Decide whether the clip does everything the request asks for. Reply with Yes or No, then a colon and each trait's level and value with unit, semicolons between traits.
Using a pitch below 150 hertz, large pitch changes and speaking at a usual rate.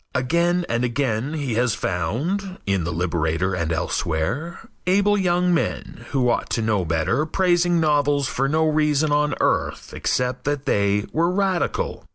Yes: medium, 140 Hz; wide, 7.9 semitones; average, 155 wpm